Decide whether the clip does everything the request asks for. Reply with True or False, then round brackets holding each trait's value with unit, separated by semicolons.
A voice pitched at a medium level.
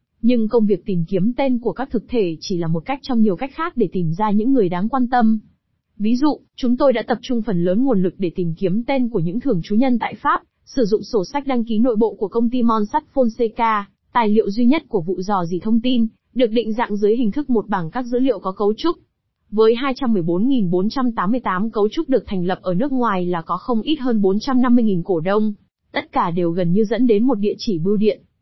False (225 Hz)